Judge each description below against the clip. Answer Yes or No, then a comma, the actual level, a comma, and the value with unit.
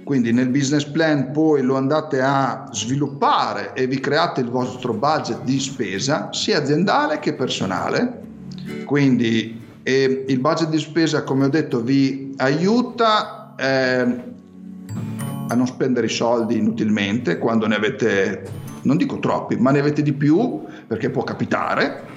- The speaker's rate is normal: Yes, average, 140 wpm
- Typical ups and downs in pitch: Yes, average, 3.4 semitones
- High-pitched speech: No, low, 135 Hz